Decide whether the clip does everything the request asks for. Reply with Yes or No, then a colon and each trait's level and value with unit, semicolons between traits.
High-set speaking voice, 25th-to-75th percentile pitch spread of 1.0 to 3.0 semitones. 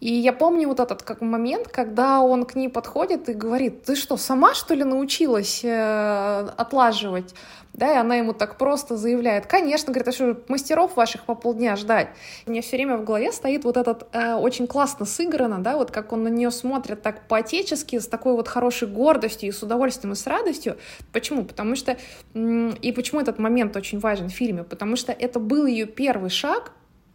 Yes: high, 240 Hz; average, 2.7 semitones